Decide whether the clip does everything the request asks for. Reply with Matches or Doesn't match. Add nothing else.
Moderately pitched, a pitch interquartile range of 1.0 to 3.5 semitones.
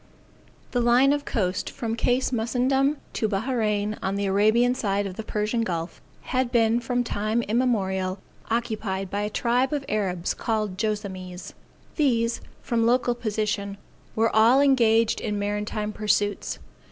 Doesn't match